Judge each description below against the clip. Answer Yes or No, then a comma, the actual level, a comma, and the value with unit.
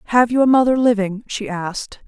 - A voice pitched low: No, high, 225 Hz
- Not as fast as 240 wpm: Yes, fast, 205 wpm